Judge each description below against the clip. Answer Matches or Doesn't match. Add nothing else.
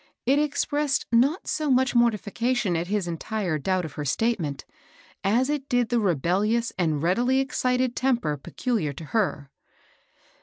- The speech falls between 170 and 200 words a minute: Doesn't match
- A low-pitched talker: Doesn't match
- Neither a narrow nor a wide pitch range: Doesn't match